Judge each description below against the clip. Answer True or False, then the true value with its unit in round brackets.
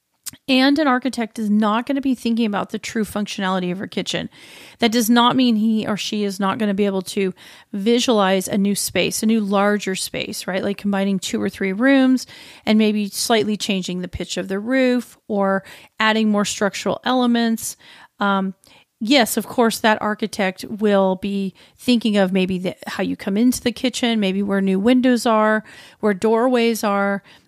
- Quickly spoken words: False (185 wpm)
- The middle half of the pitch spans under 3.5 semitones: True (3.1 semitones)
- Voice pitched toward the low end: False (210 Hz)